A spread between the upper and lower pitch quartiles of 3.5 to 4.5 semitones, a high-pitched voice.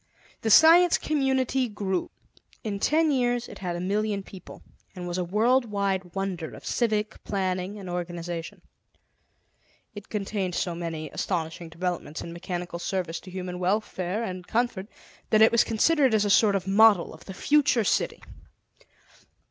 Yes: average, 3.9 semitones; high, 195 Hz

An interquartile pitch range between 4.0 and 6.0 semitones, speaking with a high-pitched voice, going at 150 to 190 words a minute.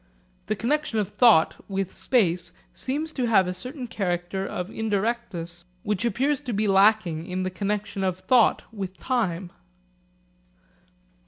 No: average, 4.3 semitones; high, 205 Hz; average, 140 wpm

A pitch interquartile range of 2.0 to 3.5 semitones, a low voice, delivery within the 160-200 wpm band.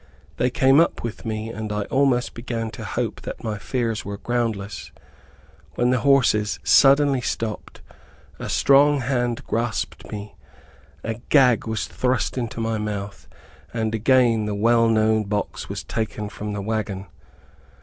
No: average, 2.8 semitones; low, 115 Hz; average, 150 wpm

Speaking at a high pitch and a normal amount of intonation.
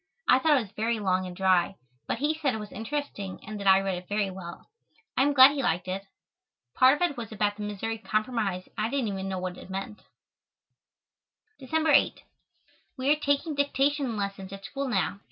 No: high, 215 Hz; wide, 6.0 semitones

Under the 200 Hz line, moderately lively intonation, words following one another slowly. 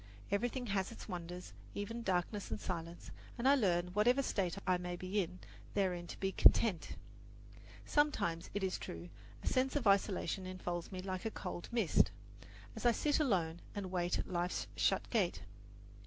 No: medium, 185 Hz; average, 4.0 semitones; average, 170 wpm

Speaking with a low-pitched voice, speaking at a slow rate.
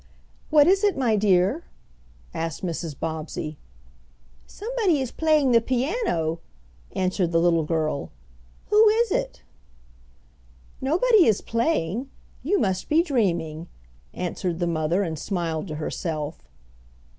No: high, 195 Hz; slow, 120 wpm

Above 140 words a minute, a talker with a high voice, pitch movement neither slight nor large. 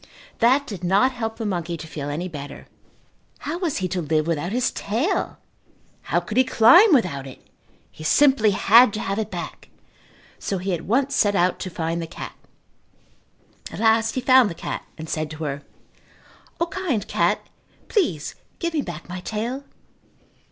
No: average, 175 wpm; high, 205 Hz; wide, 7.2 semitones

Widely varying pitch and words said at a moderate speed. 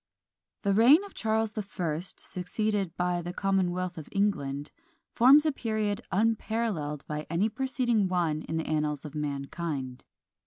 Yes: wide, 6.0 semitones; average, 145 wpm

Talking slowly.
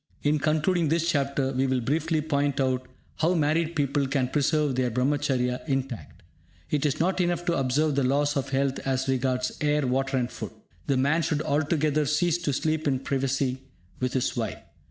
No: average, 180 wpm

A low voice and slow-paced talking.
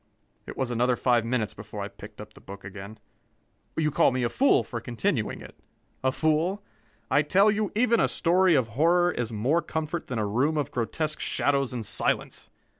No: low, 130 Hz; average, 190 wpm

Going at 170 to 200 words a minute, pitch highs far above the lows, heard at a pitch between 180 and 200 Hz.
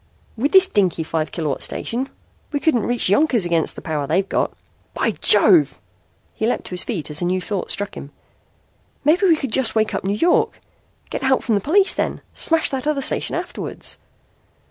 No: average, 190 wpm; wide, 8.1 semitones; high, 225 Hz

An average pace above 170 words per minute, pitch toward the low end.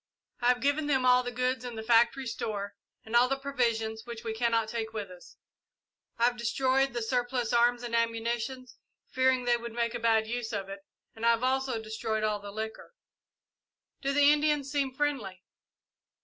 No: average, 190 wpm; high, 235 Hz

